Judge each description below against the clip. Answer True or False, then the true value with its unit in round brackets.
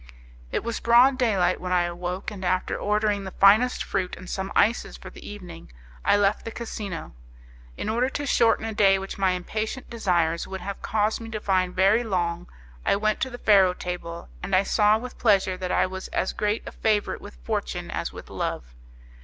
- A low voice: False (195 Hz)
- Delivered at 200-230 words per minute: True (205 wpm)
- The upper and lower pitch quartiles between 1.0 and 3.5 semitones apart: True (3.2 semitones)